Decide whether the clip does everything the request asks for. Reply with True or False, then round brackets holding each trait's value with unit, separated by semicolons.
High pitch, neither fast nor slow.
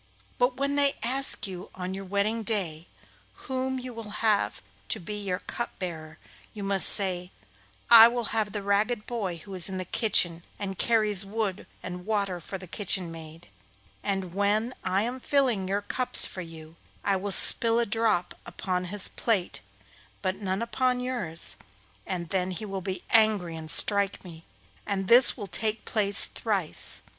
True (200 Hz; 170 wpm)